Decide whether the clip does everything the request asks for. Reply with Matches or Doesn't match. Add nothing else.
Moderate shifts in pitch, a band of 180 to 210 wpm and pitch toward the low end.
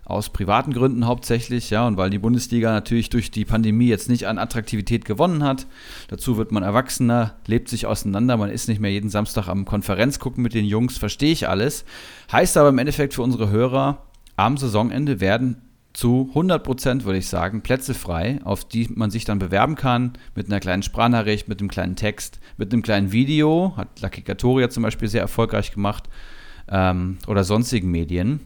Matches